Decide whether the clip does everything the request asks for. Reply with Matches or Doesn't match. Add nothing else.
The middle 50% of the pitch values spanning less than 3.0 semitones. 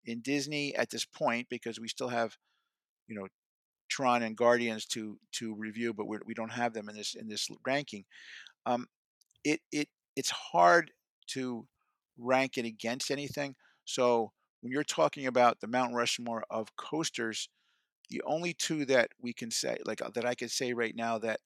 Matches